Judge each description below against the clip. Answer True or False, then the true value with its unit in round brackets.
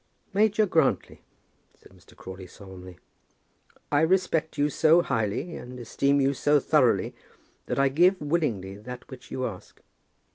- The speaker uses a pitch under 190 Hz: True (140 Hz)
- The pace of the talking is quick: False (140 wpm)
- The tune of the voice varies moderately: False (6.4 semitones)